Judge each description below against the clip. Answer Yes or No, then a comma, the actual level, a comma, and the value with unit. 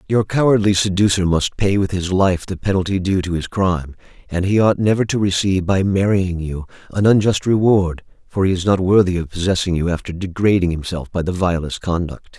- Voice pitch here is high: No, very low, 95 Hz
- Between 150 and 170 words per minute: No, average, 200 wpm